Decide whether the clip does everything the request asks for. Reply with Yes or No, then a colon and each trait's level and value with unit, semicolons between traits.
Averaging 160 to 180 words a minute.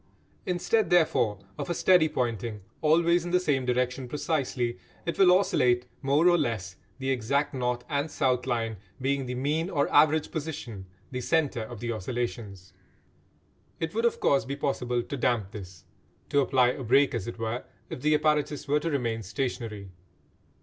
Yes: average, 170 wpm